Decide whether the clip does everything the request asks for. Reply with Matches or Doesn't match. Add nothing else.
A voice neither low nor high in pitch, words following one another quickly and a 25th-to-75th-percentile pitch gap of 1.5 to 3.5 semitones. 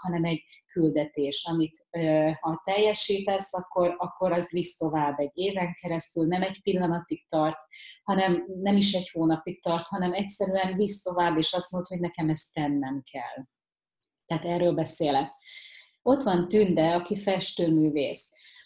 Doesn't match